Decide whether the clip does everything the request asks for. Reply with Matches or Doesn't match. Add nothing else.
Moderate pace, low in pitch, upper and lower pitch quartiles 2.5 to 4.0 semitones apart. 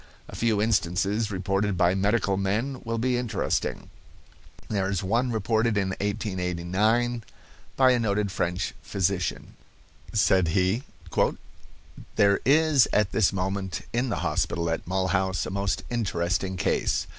Doesn't match